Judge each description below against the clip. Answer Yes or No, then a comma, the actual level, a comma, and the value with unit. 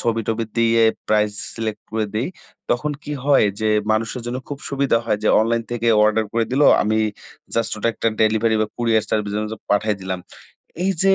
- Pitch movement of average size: No, narrow, 1.8 semitones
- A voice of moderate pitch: No, low, 115 Hz